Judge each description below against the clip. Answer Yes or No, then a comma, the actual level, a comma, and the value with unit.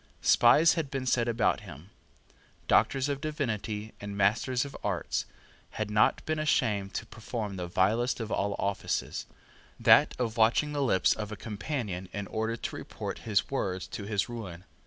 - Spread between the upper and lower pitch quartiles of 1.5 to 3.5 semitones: No, average, 4.1 semitones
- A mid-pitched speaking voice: No, low, 110 Hz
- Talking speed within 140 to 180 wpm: Yes, average, 165 wpm